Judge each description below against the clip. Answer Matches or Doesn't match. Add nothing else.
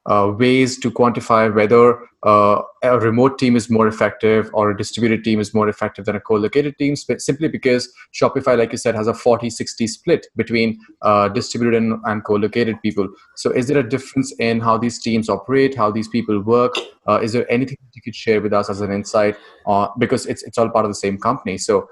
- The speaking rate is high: Matches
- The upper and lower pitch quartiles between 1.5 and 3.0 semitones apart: Matches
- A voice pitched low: Matches